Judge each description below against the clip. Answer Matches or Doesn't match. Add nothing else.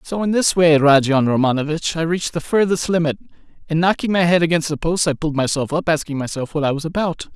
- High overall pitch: Doesn't match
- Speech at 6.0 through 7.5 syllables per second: Matches